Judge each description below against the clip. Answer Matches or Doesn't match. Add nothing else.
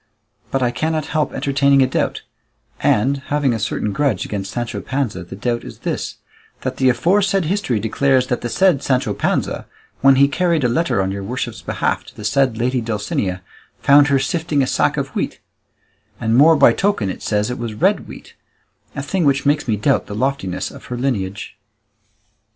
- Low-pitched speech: Matches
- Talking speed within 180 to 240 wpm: Matches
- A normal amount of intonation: Matches